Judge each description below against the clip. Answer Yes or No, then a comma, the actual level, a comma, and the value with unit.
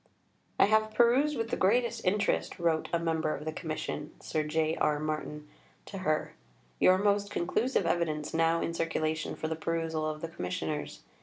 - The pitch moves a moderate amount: Yes, average, 4.1 semitones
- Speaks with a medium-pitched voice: Yes, medium, 165 Hz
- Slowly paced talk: No, average, 175 wpm